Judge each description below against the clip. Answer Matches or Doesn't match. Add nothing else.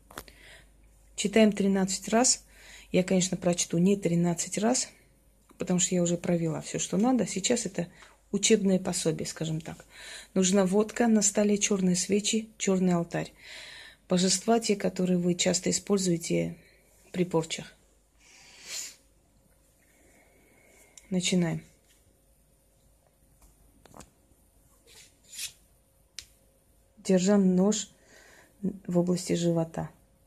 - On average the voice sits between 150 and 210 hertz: Matches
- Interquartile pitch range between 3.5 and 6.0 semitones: Doesn't match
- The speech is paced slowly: Matches